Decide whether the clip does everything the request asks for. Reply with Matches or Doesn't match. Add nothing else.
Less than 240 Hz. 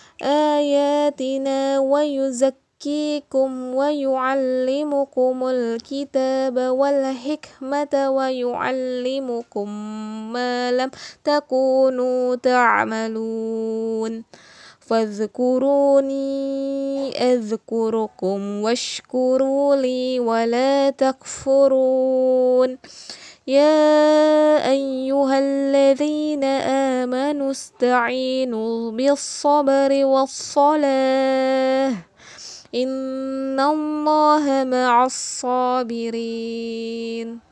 Doesn't match